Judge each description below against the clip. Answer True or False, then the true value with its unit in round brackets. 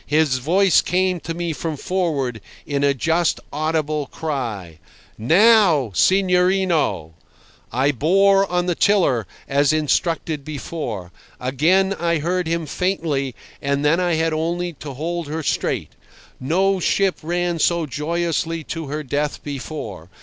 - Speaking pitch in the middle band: True (160 Hz)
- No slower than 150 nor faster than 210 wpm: False (135 wpm)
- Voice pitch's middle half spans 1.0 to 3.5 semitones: False (3.9 semitones)